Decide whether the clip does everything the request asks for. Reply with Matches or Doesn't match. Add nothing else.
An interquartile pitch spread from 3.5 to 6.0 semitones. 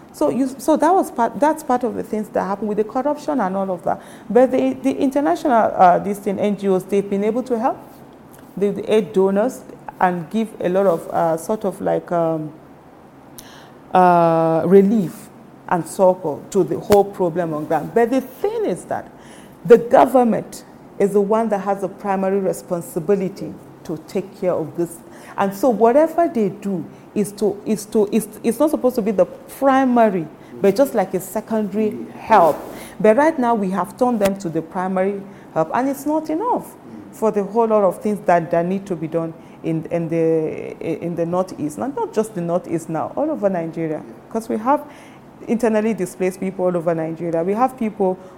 Matches